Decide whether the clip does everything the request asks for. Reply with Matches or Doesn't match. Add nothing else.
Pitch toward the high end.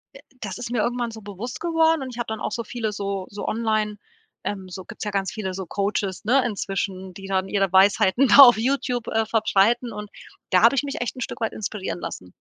Matches